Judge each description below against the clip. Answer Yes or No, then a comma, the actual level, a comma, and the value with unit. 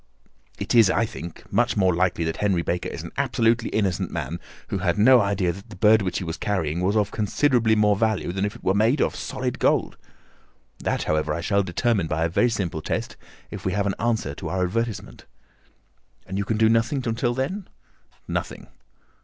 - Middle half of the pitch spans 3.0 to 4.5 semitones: Yes, average, 4.2 semitones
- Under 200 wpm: No, fast, 205 wpm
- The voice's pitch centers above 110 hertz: No, low, 100 Hz